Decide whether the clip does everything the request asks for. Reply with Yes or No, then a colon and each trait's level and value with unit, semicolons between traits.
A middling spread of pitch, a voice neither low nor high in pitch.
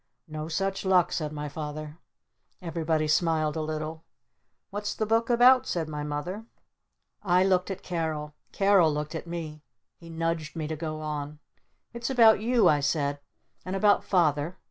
Yes: average, 3.9 semitones; medium, 160 Hz